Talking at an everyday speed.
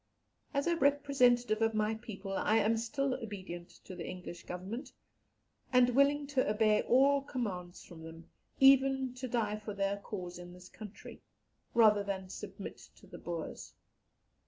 Yes: average, 155 wpm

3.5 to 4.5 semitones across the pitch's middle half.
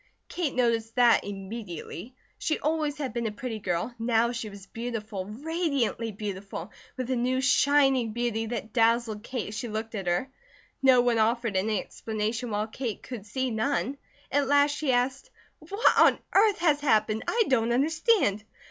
Yes: average, 3.9 semitones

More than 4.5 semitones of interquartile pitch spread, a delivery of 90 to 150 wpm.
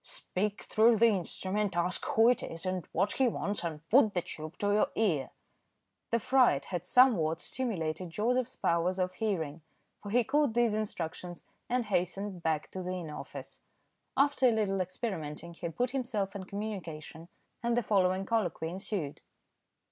No: average, 5.0 semitones; average, 165 wpm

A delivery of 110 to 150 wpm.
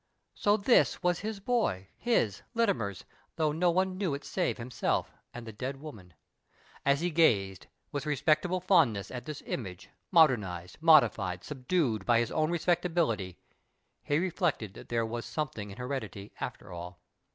No: average, 160 wpm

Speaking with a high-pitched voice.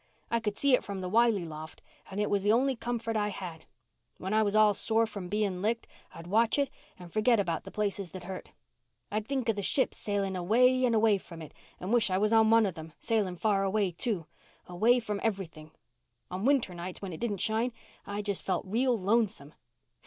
Yes: high, 205 Hz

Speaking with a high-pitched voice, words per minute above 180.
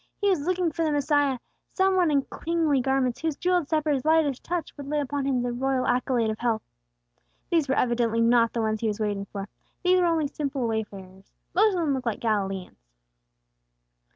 Yes: very high, 270 Hz; average, 195 wpm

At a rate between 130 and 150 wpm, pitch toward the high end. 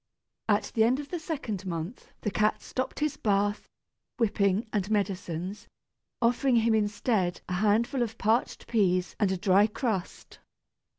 Yes: average, 145 wpm; high, 210 Hz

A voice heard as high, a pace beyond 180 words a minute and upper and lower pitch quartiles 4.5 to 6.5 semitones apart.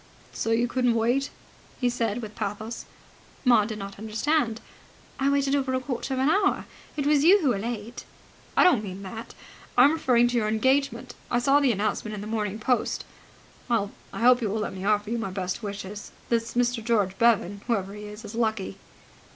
No: high, 230 Hz; average, 200 wpm; average, 3.3 semitones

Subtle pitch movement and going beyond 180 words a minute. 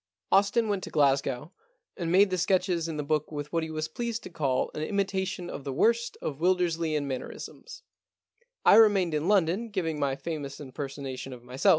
No: average, 4.9 semitones; average, 190 wpm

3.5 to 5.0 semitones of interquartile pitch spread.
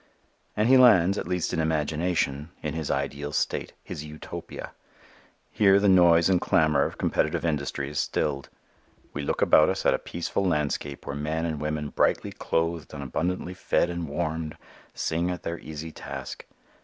No: average, 2.8 semitones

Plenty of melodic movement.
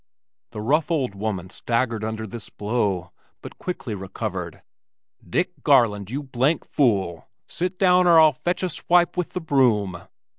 Yes: wide, 7.6 semitones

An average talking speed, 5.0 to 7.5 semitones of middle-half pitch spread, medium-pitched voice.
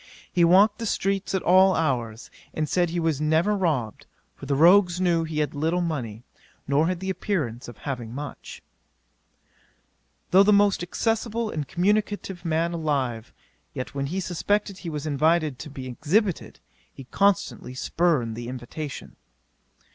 Yes: average, 155 wpm; average, 5.3 semitones; medium, 165 Hz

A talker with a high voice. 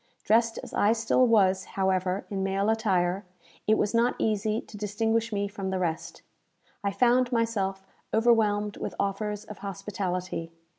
Yes: high, 205 Hz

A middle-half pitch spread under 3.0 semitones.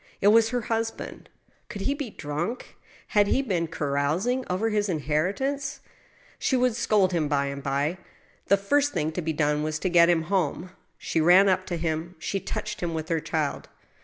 No: wide, 5.5 semitones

